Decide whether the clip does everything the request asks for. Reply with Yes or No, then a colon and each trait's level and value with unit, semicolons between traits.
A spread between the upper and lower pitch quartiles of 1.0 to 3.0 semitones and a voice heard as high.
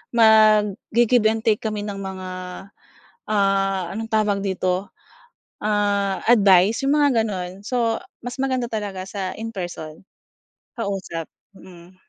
Yes: average, 2.7 semitones; high, 205 Hz